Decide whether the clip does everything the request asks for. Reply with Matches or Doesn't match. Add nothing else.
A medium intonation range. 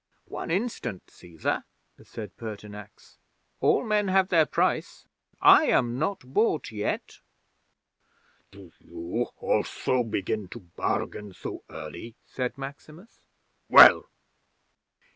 Doesn't match